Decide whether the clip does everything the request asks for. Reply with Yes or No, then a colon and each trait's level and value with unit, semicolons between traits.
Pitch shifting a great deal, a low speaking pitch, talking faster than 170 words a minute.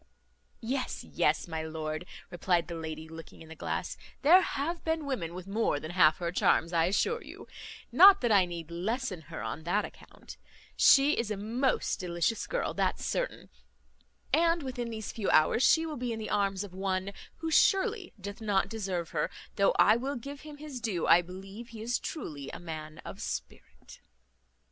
No: wide, 7.5 semitones; high, 200 Hz; average, 185 wpm